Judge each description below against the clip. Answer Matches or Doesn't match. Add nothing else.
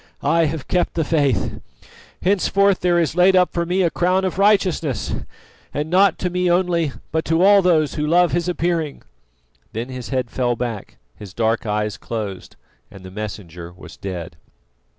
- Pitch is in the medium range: Matches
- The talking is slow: Doesn't match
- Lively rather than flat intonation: Matches